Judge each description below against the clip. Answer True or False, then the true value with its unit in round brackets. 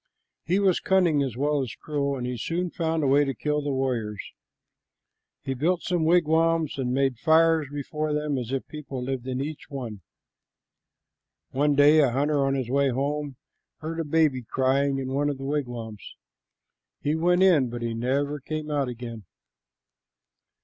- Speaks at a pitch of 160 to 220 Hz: False (140 Hz)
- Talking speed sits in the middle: True (170 wpm)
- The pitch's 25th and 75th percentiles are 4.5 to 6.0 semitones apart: False (3.0 semitones)